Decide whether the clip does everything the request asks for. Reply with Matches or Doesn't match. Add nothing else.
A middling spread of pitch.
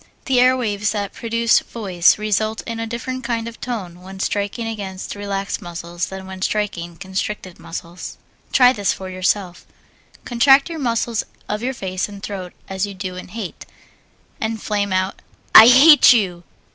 Matches